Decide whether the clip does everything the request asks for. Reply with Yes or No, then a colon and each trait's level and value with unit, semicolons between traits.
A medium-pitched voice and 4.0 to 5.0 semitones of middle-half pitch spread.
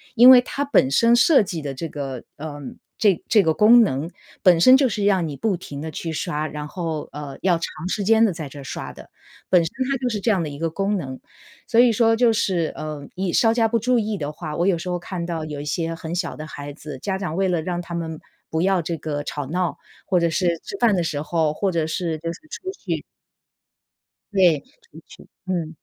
Yes: medium, 170 Hz; average, 4.7 semitones